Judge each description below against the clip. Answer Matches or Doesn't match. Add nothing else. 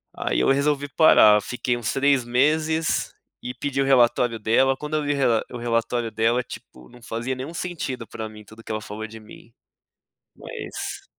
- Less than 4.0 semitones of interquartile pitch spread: Matches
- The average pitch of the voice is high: Doesn't match